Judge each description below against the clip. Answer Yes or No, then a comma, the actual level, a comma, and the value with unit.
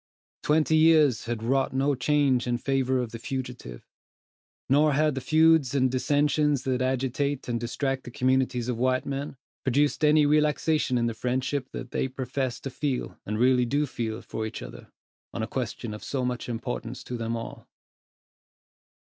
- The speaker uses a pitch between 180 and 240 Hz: No, low, 130 Hz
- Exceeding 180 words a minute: No, average, 170 wpm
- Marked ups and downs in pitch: No, average, 2.8 semitones